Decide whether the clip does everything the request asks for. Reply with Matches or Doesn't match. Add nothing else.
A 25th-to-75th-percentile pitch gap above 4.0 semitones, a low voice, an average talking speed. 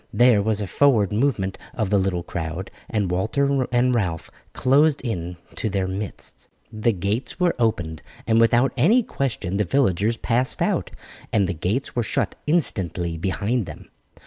Matches